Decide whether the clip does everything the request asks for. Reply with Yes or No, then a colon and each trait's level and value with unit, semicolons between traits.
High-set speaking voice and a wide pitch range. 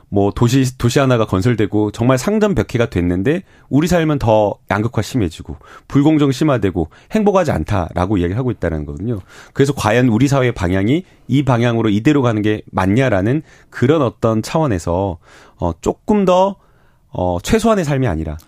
No: low, 120 Hz; wide, 6.2 semitones